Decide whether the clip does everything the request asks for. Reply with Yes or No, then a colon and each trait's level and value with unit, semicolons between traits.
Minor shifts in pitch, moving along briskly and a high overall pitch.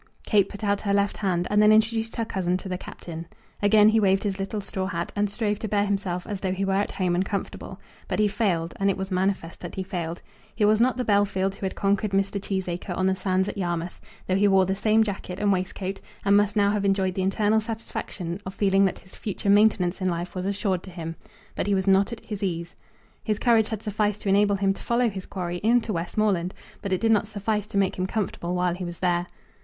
Yes: narrow, 2.0 semitones; fast, 245 wpm; high, 195 Hz